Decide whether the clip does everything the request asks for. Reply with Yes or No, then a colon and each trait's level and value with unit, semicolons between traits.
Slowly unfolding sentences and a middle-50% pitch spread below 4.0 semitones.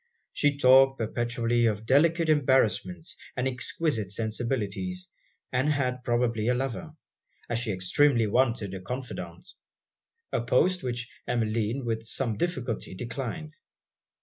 Yes: slow, 120 wpm; average, 3.4 semitones